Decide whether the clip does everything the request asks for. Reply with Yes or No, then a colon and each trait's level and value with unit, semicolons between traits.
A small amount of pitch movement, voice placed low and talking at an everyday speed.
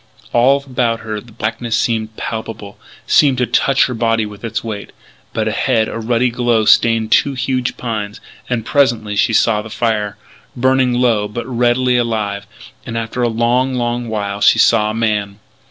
Yes: narrow, 2.1 semitones; low, 115 Hz; average, 170 wpm